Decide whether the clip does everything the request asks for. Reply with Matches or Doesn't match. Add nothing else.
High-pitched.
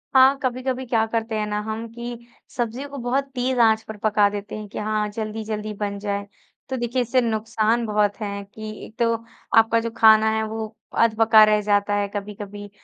Matches